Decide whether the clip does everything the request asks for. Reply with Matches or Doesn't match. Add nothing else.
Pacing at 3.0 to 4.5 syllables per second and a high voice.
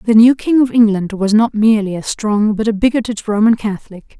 Doesn't match